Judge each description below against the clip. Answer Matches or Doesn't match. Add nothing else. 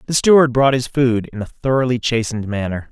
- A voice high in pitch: Doesn't match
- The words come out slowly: Doesn't match